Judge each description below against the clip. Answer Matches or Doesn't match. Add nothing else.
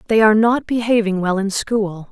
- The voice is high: Matches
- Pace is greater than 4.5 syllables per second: Matches